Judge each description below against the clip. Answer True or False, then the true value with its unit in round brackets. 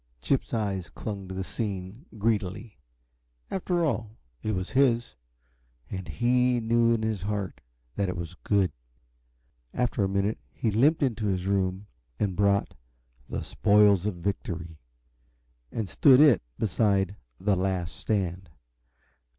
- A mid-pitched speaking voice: False (100 Hz)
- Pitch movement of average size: True (3.5 semitones)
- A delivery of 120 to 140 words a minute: True (135 wpm)